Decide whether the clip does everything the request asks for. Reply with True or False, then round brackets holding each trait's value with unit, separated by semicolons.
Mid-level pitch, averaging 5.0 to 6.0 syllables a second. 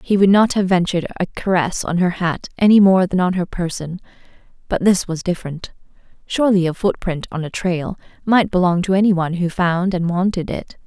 True (180 Hz; 5.6 syllables/s)